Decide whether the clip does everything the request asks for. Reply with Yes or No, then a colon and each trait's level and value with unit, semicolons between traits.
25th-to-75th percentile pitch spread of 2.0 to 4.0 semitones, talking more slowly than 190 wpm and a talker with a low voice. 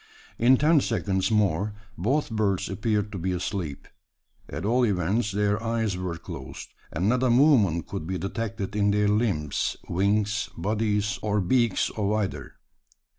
Yes: average, 3.2 semitones; average, 150 wpm; low, 105 Hz